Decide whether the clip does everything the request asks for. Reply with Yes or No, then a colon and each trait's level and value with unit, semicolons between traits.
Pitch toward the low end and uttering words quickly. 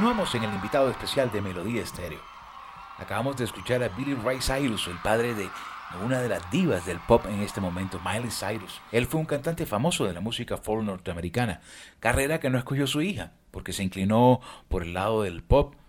Yes: low, 110 Hz; fast, 200 wpm